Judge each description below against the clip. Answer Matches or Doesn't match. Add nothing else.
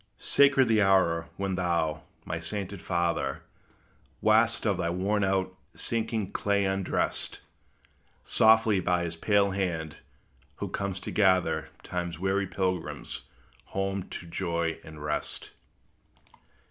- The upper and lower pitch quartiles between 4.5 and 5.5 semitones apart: Doesn't match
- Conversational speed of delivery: Doesn't match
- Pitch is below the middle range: Matches